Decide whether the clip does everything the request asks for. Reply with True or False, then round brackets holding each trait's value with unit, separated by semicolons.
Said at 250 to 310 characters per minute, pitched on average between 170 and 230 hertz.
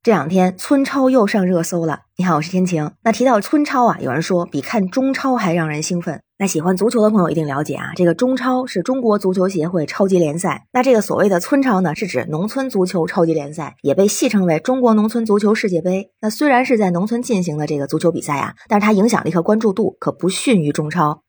False (360 characters per minute; 185 Hz)